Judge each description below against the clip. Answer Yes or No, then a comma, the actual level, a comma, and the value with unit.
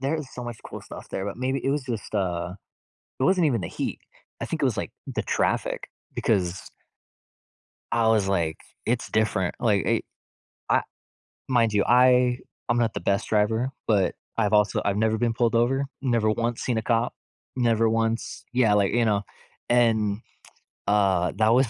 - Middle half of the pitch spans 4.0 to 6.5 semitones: No, average, 2.9 semitones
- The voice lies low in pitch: Yes, low, 115 Hz